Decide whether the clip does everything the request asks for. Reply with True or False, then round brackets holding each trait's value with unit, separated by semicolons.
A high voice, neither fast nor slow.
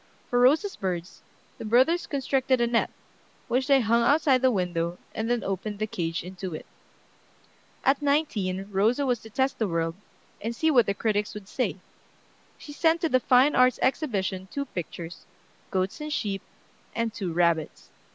True (230 Hz; 170 wpm)